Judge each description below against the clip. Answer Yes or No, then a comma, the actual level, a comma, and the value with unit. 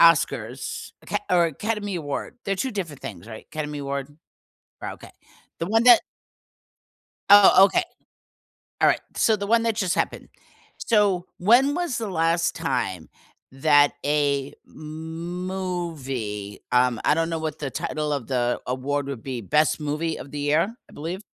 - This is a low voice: No, medium, 155 Hz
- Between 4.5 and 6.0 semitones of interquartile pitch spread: Yes, average, 5.3 semitones